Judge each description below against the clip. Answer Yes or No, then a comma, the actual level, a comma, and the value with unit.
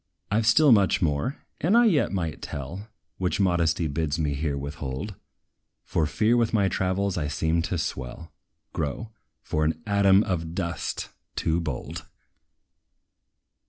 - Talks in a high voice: No, very low, 85 Hz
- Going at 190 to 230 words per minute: No, average, 145 wpm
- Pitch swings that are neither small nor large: Yes, average, 4.8 semitones